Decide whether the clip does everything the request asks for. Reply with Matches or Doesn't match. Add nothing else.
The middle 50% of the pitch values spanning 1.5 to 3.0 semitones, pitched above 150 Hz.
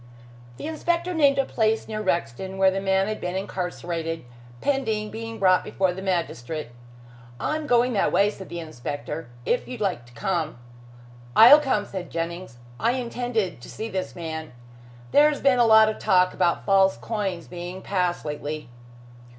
Doesn't match